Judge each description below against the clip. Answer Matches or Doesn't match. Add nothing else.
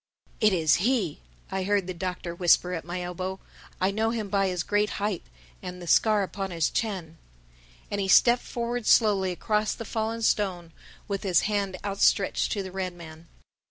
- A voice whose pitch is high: Matches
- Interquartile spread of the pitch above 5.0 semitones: Doesn't match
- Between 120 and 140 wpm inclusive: Doesn't match